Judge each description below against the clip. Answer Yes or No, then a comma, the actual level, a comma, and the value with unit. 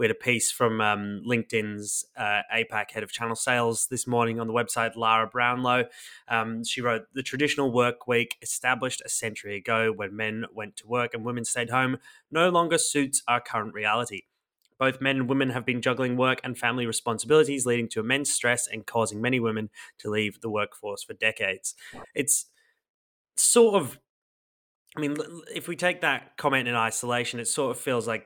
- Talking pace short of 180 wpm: No, average, 185 wpm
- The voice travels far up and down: No, average, 2.8 semitones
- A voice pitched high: No, low, 120 Hz